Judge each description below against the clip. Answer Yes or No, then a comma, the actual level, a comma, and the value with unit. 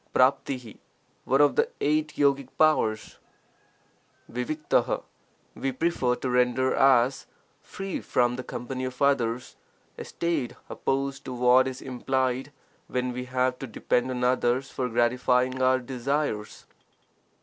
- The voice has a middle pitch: No, low, 130 Hz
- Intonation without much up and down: Yes, narrow, 1.7 semitones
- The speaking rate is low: Yes, slow, 130 wpm